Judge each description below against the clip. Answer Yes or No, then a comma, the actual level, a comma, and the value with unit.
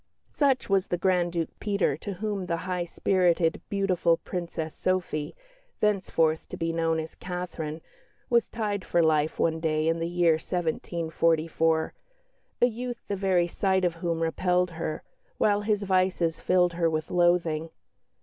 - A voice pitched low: No, medium, 175 Hz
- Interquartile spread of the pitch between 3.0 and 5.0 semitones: No, narrow, 2.6 semitones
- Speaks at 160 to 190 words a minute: No, average, 150 wpm